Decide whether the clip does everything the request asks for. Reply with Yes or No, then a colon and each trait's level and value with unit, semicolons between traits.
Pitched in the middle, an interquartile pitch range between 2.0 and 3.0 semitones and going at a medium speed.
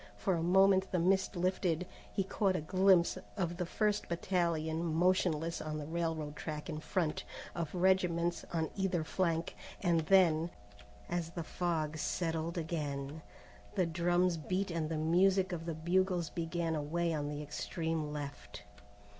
Yes: medium, 170 Hz; narrow, 2.5 semitones; average, 150 wpm